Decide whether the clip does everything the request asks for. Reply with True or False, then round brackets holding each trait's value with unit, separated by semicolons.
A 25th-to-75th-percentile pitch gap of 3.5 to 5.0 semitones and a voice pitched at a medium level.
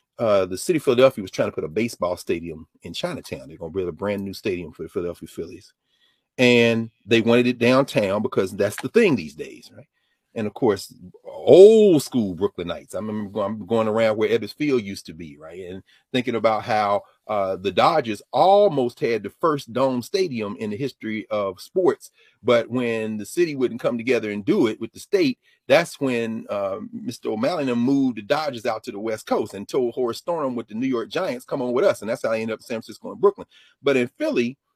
False (4.2 semitones; 120 Hz)